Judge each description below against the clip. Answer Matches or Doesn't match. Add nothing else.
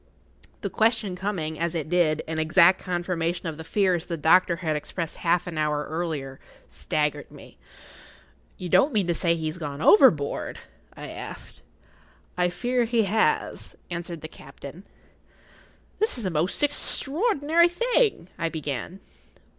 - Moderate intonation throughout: Matches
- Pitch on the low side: Doesn't match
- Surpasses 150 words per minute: Doesn't match